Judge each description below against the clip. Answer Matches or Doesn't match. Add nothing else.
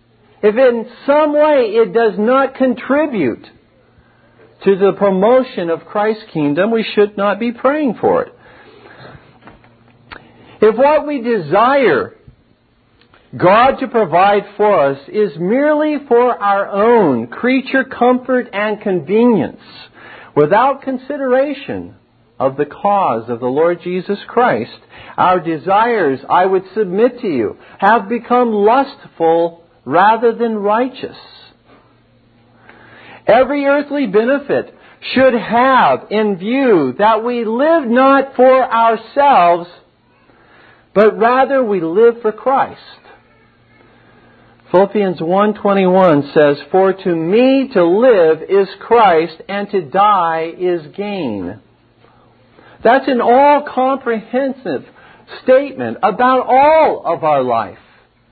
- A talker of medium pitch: Doesn't match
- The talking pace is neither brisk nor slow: Doesn't match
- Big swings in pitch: Matches